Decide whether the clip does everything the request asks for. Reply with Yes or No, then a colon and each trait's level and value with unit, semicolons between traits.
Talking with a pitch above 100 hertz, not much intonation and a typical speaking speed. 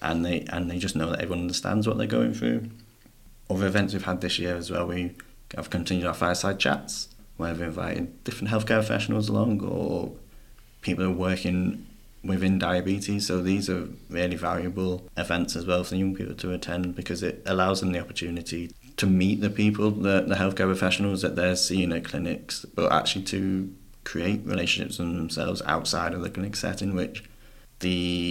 No: very low, 95 Hz; narrow, 2.2 semitones; average, 185 wpm